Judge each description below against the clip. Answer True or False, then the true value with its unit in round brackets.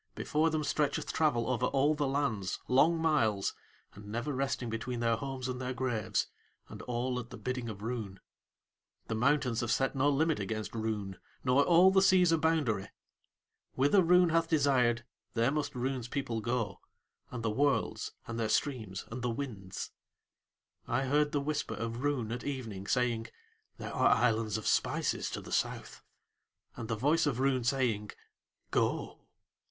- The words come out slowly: False (165 wpm)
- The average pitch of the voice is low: True (125 Hz)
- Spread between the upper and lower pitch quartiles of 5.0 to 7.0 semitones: False (4.1 semitones)